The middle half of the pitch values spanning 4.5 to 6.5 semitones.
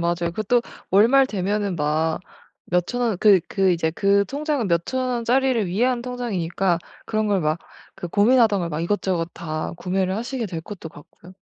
Yes: wide, 5.4 semitones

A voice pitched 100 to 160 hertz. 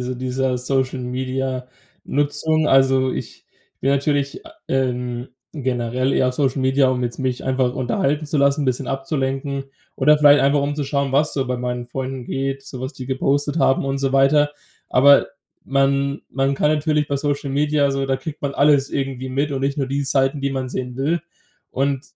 Yes: low, 135 Hz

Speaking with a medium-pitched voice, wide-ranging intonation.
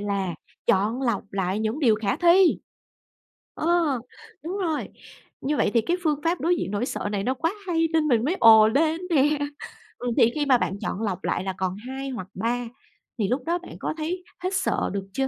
No: very high, 260 Hz; wide, 7.4 semitones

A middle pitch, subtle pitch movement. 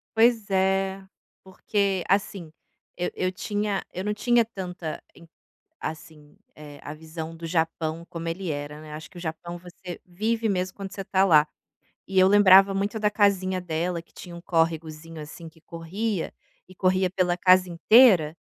No: medium, 180 Hz; average, 3.0 semitones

